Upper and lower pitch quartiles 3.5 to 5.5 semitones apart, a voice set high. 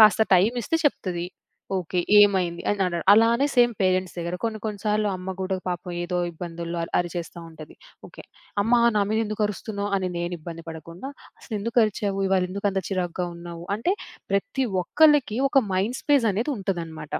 Yes: average, 3.9 semitones; high, 195 Hz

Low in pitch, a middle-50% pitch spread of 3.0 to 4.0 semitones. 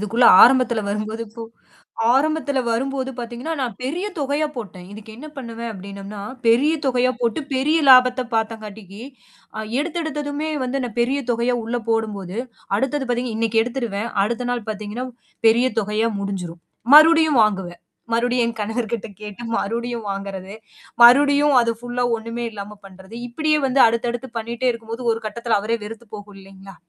No: high, 235 Hz; average, 3.3 semitones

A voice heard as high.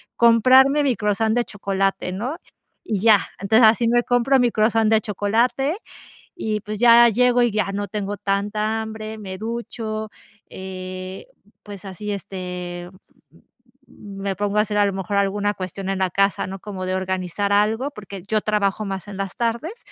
Yes: high, 210 Hz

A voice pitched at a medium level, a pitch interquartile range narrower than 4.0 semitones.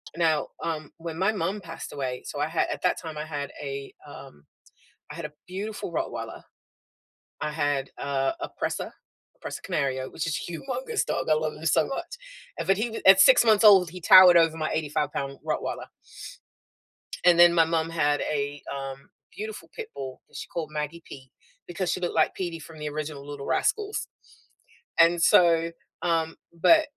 Yes: medium, 160 Hz; average, 3.4 semitones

